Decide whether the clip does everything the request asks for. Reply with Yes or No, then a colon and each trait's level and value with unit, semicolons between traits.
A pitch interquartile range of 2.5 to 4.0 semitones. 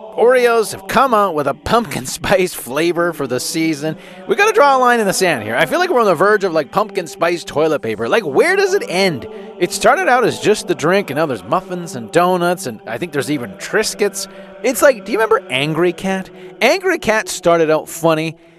No: average, 4.5 semitones